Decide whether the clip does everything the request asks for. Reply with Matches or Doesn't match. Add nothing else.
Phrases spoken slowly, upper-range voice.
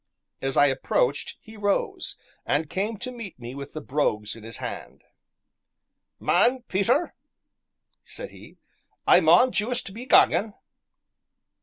Matches